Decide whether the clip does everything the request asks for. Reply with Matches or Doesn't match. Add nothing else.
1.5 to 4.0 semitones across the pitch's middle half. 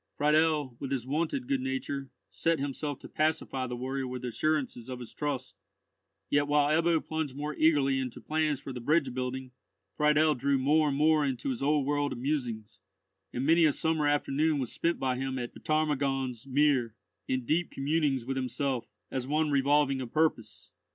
Matches